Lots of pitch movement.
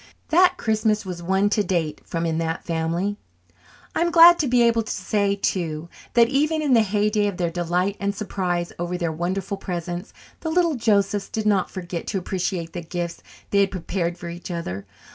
No: average, 3.7 semitones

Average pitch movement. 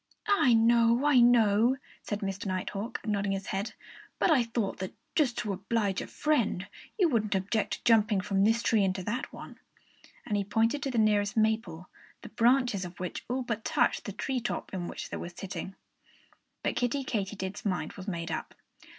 Yes: average, 3.5 semitones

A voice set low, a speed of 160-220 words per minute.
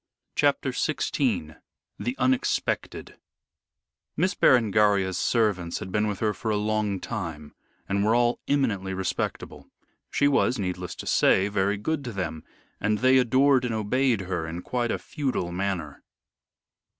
No: low, 105 Hz; average, 140 wpm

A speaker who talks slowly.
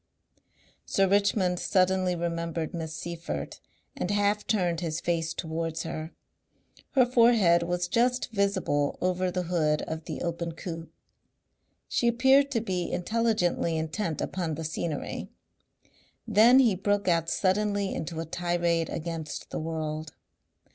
Yes: slow, 130 wpm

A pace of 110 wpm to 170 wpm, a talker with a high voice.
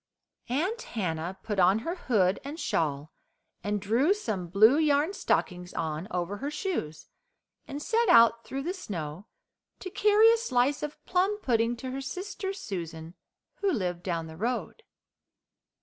Yes: average, 150 wpm; high, 230 Hz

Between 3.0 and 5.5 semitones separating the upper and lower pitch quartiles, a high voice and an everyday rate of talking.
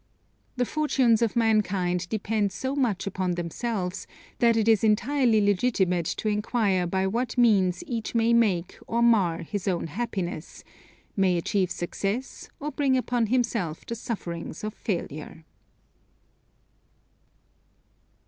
No: average, 4.5 semitones; high, 210 Hz; slow, 125 wpm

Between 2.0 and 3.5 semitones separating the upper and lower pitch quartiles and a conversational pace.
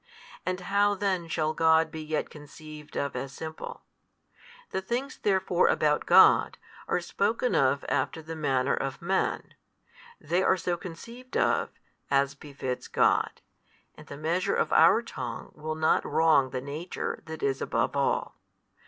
No: average, 4.1 semitones; average, 150 wpm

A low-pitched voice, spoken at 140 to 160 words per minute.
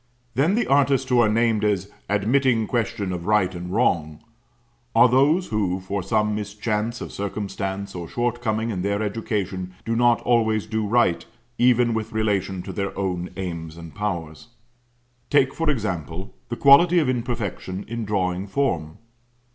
Yes: low, 105 Hz; average, 155 wpm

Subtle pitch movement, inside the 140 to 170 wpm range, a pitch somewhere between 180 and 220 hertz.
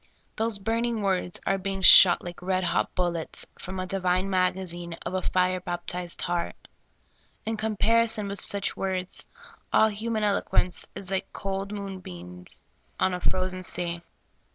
Yes: narrow, 2.0 semitones; average, 145 wpm; medium, 185 Hz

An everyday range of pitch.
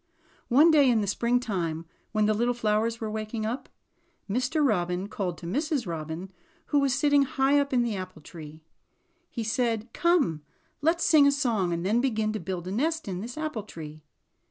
No: wide, 6.4 semitones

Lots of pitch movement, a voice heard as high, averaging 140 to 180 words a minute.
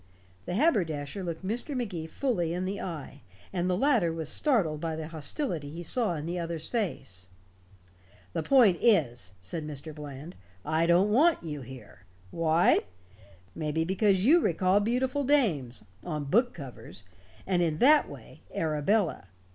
No: wide, 5.7 semitones; medium, 170 Hz; average, 150 wpm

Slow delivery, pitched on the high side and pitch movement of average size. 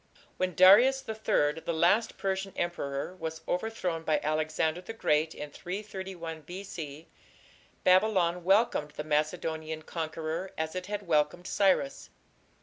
No: slow, 125 wpm; medium, 175 Hz; average, 3.4 semitones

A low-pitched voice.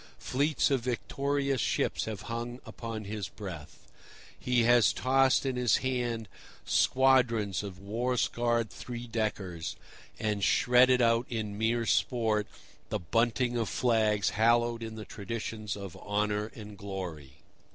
Yes: low, 115 Hz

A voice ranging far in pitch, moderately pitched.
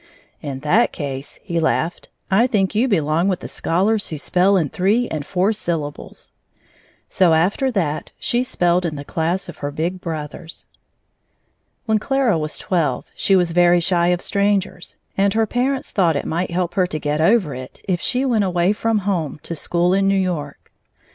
No: average, 3.9 semitones; medium, 180 Hz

